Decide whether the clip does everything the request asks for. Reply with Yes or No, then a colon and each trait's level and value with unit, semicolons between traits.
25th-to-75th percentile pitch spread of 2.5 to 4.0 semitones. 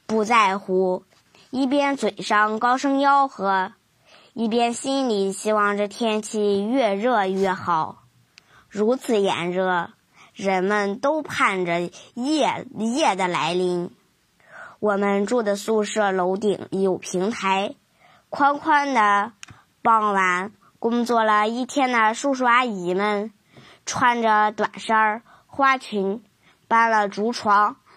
Yes: average, 3.5 semitones